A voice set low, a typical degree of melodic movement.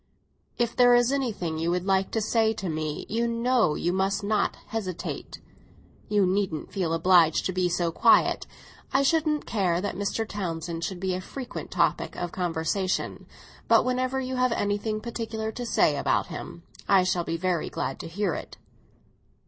No: high, 195 Hz; average, 4.7 semitones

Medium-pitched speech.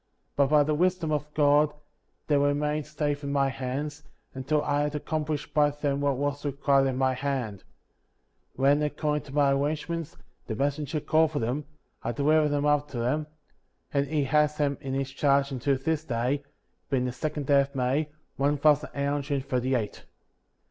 Yes: medium, 145 Hz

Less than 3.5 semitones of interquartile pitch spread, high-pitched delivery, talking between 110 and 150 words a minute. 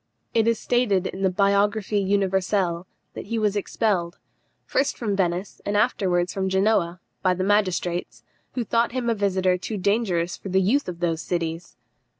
No: average, 2.7 semitones; high, 195 Hz; average, 165 wpm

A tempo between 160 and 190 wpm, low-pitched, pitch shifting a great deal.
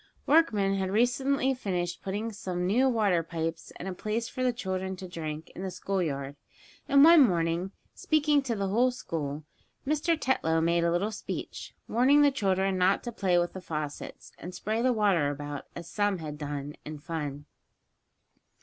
No: average, 175 wpm; high, 190 Hz; wide, 6.1 semitones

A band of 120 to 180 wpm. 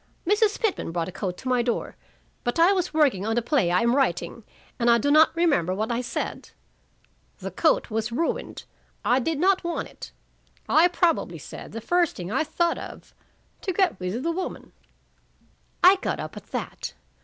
No: average, 190 wpm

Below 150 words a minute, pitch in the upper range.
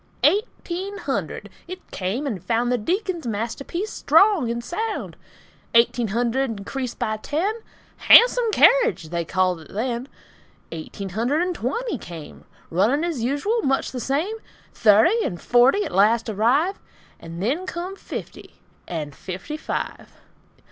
Yes: slow, 135 wpm; very high, 250 Hz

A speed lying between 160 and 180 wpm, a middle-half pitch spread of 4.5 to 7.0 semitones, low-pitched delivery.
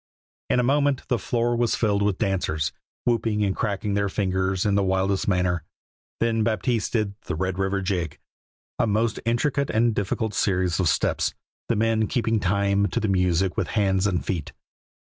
No: average, 175 wpm; average, 3.2 semitones; low, 100 Hz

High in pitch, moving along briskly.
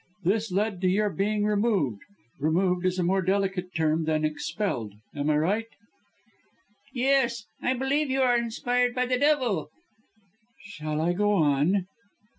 No: high, 195 Hz; average, 145 wpm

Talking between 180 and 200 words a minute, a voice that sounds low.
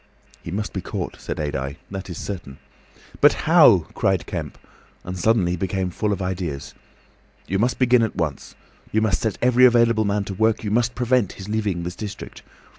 Yes: average, 185 wpm; low, 100 Hz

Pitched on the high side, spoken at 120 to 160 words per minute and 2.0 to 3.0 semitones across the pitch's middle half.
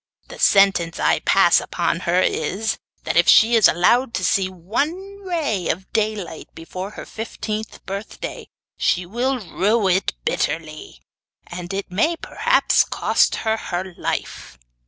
No: high, 195 Hz; average, 140 wpm; average, 4.4 semitones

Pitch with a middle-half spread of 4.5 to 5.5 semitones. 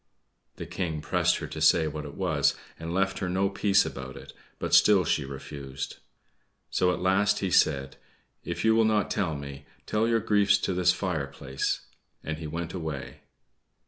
Yes: average, 5.2 semitones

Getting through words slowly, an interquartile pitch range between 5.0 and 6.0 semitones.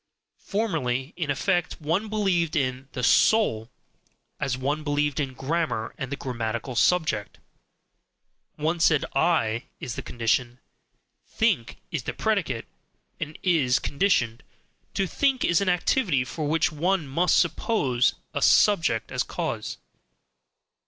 Yes: slow, 125 wpm; wide, 5.6 semitones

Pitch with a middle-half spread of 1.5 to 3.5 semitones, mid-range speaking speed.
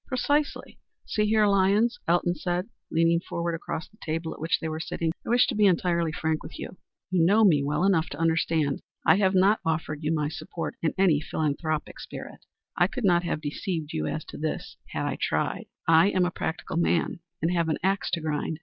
No: average, 3.2 semitones; fast, 215 wpm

